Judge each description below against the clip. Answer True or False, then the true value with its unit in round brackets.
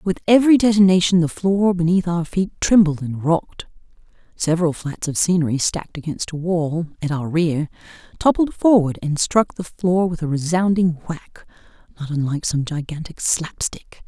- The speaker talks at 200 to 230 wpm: False (160 wpm)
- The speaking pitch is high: False (170 Hz)